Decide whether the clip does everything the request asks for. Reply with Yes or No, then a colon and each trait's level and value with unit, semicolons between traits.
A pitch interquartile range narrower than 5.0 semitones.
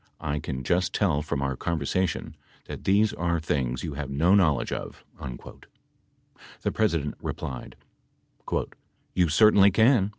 No: average, 5.3 semitones